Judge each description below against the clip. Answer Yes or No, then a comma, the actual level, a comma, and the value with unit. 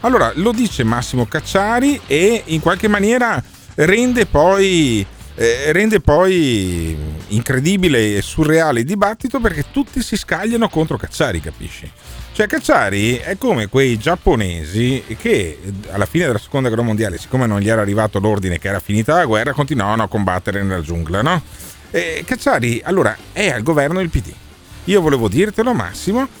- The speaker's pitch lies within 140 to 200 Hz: No, low, 130 Hz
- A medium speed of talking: Yes, average, 155 wpm